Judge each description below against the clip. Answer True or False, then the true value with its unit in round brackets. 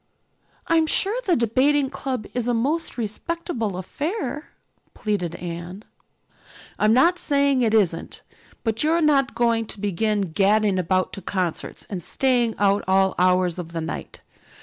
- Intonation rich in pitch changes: True (6.5 semitones)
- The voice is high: True (220 Hz)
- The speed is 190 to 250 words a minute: False (145 wpm)